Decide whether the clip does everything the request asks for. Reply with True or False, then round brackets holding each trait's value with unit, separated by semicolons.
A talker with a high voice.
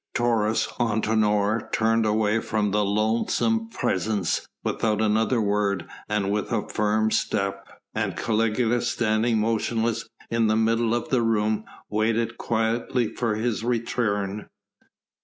False (110 Hz)